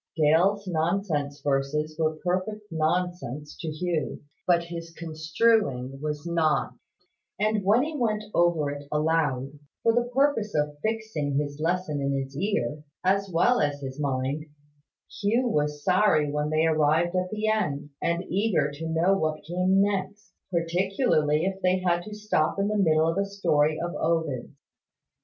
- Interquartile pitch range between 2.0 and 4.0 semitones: No, average, 4.7 semitones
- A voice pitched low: No, medium, 165 Hz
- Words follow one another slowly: No, average, 155 wpm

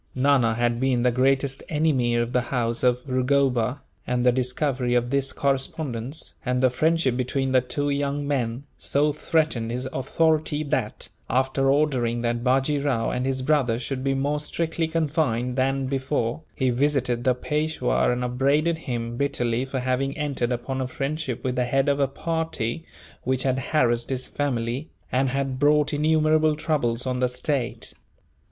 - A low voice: Yes, low, 130 Hz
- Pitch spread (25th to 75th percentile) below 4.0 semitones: Yes, average, 2.7 semitones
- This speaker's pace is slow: No, average, 165 wpm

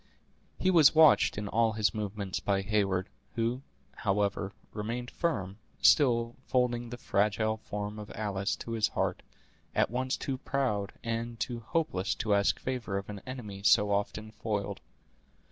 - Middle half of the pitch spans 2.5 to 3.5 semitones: Yes, average, 3.1 semitones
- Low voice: Yes, low, 110 Hz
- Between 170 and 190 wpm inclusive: No, average, 150 wpm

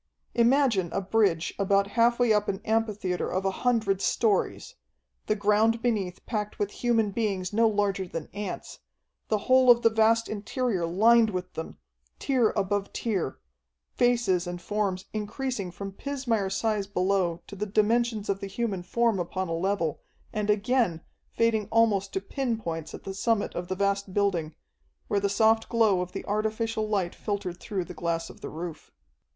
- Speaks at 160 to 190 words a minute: Yes, average, 170 wpm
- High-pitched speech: Yes, high, 205 Hz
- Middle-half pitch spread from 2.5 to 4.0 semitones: Yes, average, 3.2 semitones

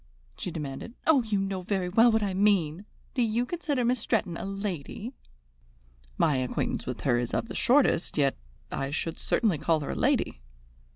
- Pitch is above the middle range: Yes, high, 195 Hz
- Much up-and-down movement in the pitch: Yes, wide, 6.9 semitones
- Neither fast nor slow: Yes, average, 180 wpm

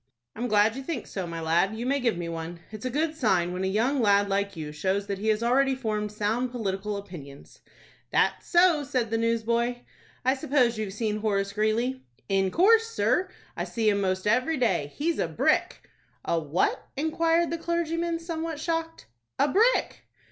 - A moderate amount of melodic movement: No, wide, 6.5 semitones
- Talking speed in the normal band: Yes, average, 185 wpm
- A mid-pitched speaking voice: No, high, 225 Hz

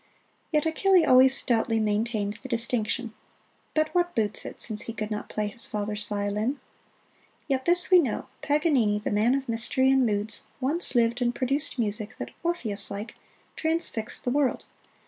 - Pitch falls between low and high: No, high, 240 Hz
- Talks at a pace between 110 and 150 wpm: No, average, 165 wpm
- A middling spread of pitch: Yes, average, 4.7 semitones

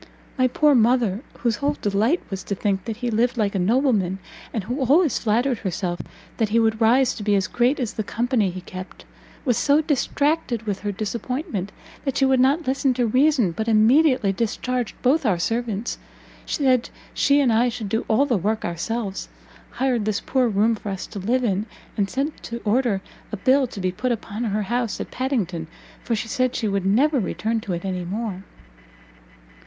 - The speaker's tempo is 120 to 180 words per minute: No, average, 195 wpm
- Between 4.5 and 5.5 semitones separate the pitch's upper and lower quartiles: No, average, 4.1 semitones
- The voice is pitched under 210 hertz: No, high, 230 Hz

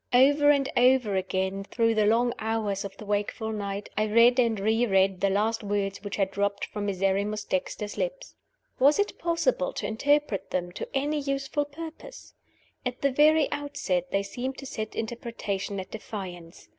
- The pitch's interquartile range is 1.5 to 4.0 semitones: No, average, 5.3 semitones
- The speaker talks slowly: No, average, 170 wpm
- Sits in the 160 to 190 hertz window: No, high, 220 Hz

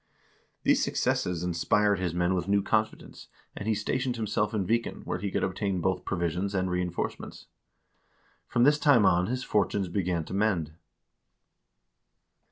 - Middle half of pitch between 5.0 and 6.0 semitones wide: No, average, 3.3 semitones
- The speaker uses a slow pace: No, average, 150 wpm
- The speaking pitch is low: Yes, low, 100 Hz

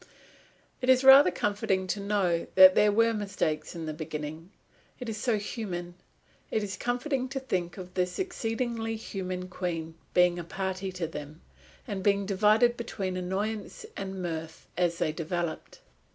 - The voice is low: No, high, 190 Hz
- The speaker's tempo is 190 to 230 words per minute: No, average, 155 wpm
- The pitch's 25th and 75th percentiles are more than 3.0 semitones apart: Yes, average, 4.0 semitones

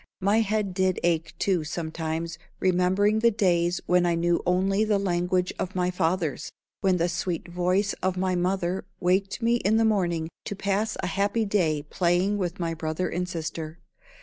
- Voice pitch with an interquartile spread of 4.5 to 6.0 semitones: No, narrow, 2.4 semitones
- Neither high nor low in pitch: Yes, medium, 180 Hz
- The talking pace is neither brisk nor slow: Yes, average, 175 wpm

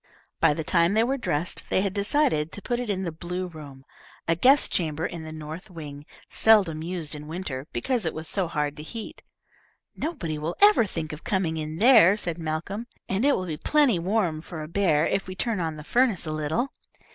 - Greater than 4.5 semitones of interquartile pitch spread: Yes, average, 5.0 semitones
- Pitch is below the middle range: No, medium, 170 Hz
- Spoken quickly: Yes, fast, 215 wpm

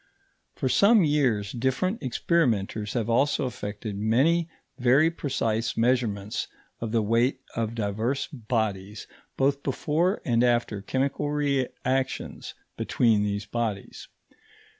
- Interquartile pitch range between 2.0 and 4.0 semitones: No, average, 4.4 semitones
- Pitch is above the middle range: No, low, 120 Hz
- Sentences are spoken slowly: Yes, slow, 110 wpm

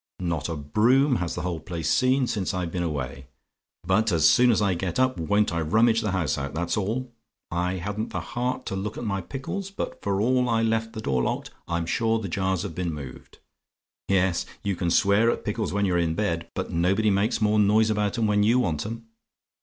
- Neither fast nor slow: No, fast, 220 wpm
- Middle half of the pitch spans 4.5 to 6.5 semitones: Yes, average, 4.8 semitones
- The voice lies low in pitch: Yes, low, 100 Hz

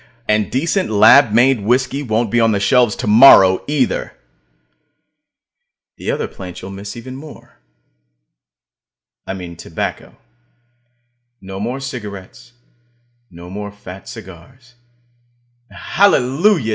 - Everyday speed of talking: No, slow, 110 wpm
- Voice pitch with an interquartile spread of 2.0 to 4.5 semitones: No, average, 4.9 semitones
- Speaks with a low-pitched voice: Yes, low, 115 Hz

